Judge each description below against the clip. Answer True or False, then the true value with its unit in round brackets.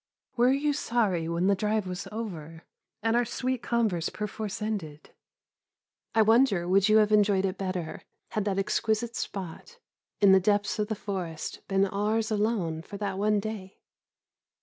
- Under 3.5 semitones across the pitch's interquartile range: True (2.8 semitones)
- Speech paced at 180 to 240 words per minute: False (160 wpm)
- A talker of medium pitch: False (205 Hz)